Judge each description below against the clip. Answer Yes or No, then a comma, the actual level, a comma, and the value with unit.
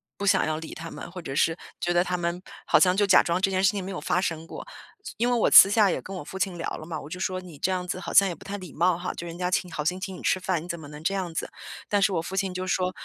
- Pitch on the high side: No, medium, 180 Hz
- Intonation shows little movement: Yes, narrow, 2.0 semitones